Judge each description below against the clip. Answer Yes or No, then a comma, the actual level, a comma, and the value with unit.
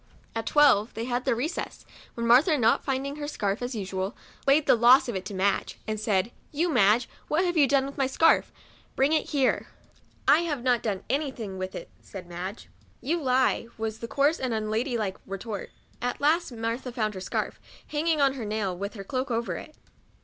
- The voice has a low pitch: No, high, 240 Hz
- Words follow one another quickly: Yes, fast, 210 wpm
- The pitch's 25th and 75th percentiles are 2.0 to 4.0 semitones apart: No, average, 4.7 semitones